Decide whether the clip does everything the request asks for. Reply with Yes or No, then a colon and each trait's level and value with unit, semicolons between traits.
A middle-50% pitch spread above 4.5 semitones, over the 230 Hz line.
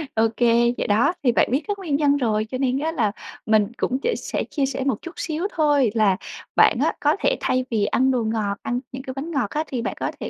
No: average, 4.2 semitones; very high, 255 Hz